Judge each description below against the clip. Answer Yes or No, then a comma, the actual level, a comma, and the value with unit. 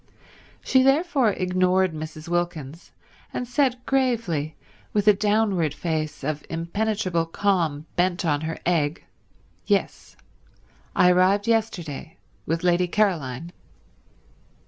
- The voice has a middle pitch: Yes, medium, 180 Hz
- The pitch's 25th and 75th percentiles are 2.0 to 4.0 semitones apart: No, average, 4.7 semitones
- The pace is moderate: No, slow, 105 wpm